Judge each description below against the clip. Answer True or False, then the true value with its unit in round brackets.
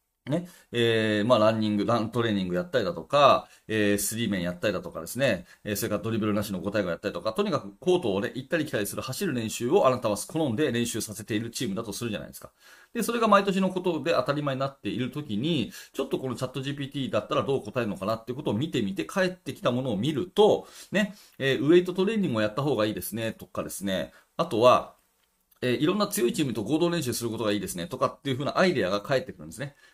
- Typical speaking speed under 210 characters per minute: False (535 characters per minute)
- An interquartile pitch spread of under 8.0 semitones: True (6.8 semitones)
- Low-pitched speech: True (120 Hz)